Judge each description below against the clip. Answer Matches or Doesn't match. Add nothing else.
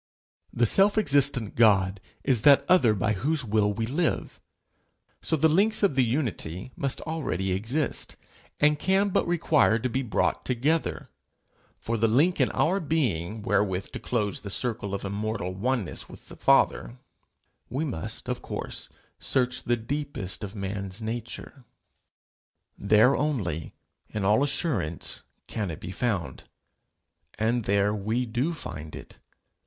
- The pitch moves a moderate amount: Doesn't match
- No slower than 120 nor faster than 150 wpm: Matches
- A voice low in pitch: Matches